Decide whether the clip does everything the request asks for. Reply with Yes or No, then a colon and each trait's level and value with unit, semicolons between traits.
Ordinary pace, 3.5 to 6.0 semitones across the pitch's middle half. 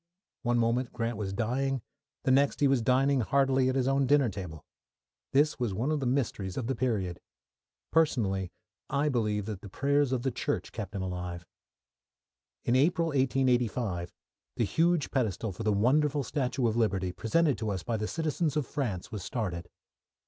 Yes: average, 170 wpm; average, 4.8 semitones